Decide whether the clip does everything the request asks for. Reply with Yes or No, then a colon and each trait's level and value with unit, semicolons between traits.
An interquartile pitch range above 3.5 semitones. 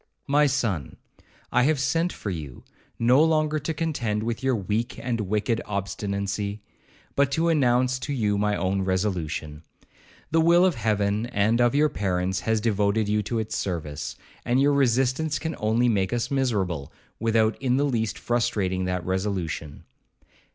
Yes: average, 5.0 semitones